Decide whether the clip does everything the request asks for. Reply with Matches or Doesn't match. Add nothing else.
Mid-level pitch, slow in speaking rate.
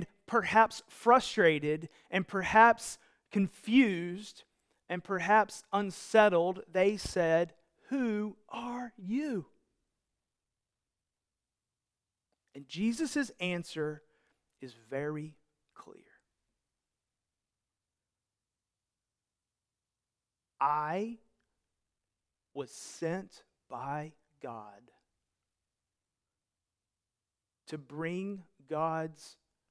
Matches